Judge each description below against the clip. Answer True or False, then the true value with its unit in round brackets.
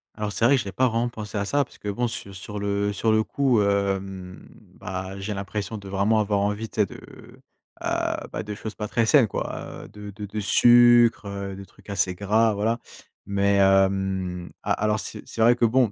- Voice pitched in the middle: False (105 Hz)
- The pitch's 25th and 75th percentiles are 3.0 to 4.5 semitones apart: False (2.4 semitones)